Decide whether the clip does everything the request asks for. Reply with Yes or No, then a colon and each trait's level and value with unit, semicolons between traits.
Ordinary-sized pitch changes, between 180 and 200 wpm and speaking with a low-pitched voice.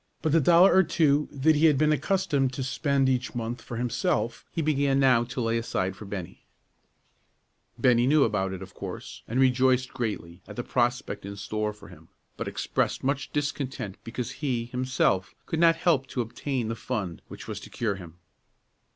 Yes: average, 4.3 semitones; average, 185 wpm; low, 125 Hz